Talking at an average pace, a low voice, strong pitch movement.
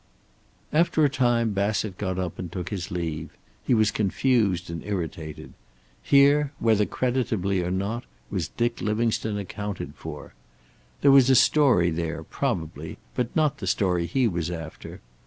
Yes: average, 150 wpm; low, 100 Hz; wide, 5.7 semitones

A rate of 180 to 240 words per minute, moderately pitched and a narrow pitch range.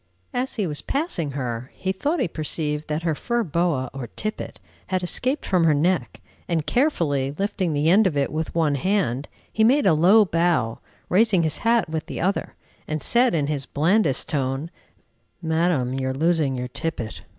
No: average, 185 wpm; medium, 165 Hz; average, 5.1 semitones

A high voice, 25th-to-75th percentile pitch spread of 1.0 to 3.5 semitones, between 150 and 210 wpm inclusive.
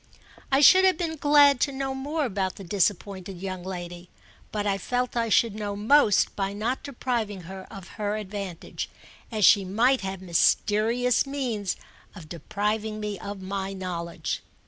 No: high, 205 Hz; average, 4.6 semitones; average, 160 wpm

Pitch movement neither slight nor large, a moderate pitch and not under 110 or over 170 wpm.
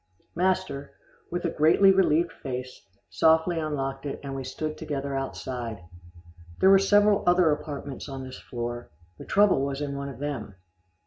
Yes: average, 4.3 semitones; medium, 145 Hz; average, 155 wpm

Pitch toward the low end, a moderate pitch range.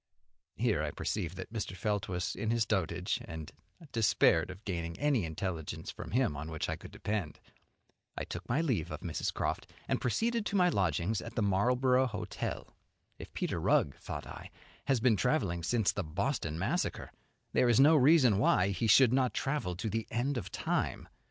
No: low, 105 Hz; wide, 6.3 semitones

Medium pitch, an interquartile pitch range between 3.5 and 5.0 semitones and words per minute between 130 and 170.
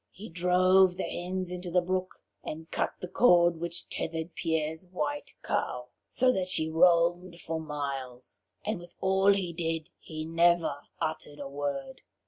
No: medium, 170 Hz; narrow, 2.5 semitones; average, 155 wpm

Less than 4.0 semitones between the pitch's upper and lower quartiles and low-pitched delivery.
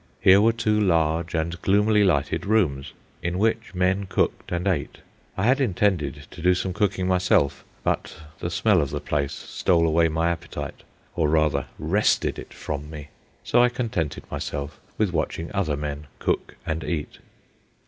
No: average, 4.6 semitones; very low, 85 Hz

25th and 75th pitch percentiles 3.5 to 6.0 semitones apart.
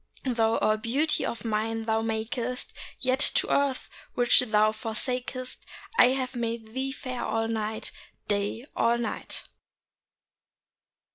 No: narrow, 2.5 semitones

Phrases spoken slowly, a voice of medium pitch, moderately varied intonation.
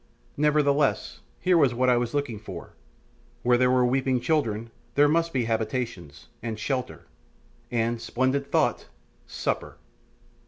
No: slow, 130 wpm; low, 125 Hz; average, 3.4 semitones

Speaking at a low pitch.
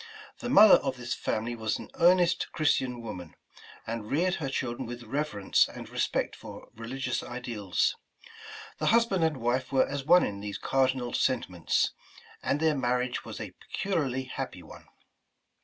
Yes: low, 130 Hz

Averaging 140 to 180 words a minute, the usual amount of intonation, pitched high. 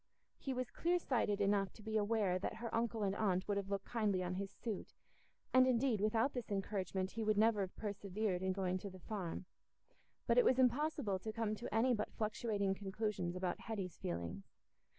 No: average, 195 wpm; average, 3.1 semitones; high, 210 Hz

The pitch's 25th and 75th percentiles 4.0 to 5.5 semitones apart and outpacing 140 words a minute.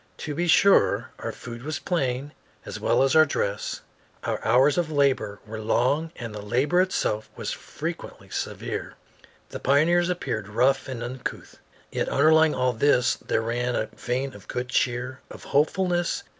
Yes: average, 4.5 semitones; average, 160 wpm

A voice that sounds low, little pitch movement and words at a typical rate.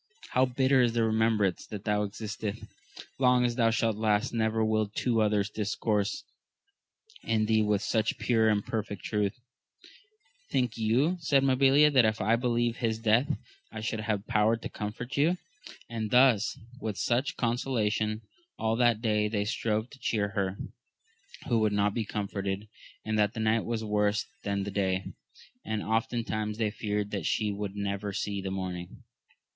Yes: low, 110 Hz; narrow, 2.1 semitones; average, 165 wpm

